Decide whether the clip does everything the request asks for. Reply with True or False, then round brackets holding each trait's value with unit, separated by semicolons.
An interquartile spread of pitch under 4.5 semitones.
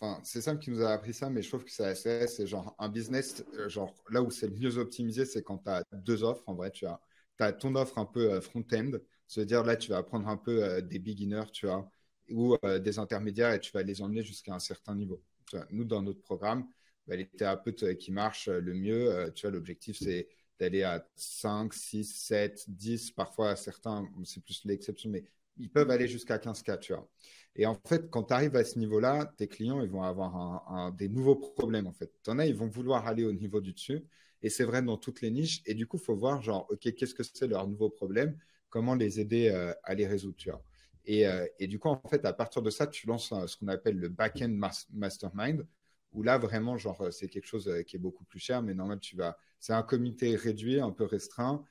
True (3.6 semitones)